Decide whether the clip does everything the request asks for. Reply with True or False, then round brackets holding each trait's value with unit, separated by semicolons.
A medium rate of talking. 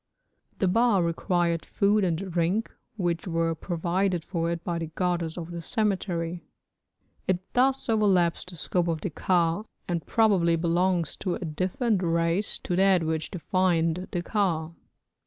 True (150 wpm)